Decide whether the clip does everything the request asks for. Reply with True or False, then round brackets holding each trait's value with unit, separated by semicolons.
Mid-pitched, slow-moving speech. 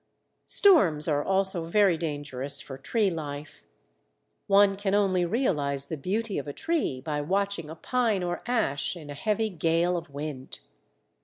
False (170 Hz; 155 wpm)